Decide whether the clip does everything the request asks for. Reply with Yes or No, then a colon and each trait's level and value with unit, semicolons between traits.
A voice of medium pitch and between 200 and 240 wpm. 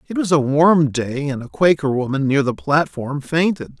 Yes: medium, 150 Hz; fast, 205 wpm